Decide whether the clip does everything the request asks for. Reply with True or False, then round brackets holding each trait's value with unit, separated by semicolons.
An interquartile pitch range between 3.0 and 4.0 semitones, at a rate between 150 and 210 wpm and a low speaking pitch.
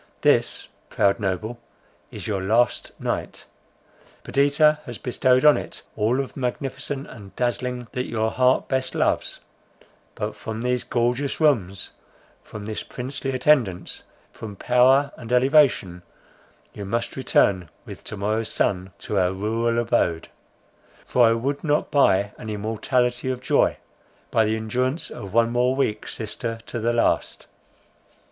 False (3.3 semitones; 140 wpm; 120 Hz)